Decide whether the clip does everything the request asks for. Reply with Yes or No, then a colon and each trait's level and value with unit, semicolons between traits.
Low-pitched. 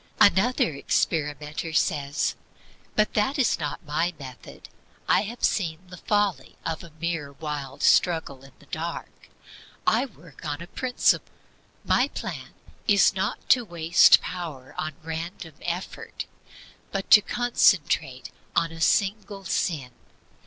No: medium, 170 Hz